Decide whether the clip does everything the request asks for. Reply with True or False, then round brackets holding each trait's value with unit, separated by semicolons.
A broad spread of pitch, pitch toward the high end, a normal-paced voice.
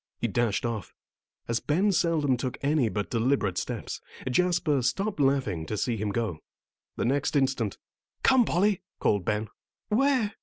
False (7.5 semitones; 130 Hz; 150 wpm)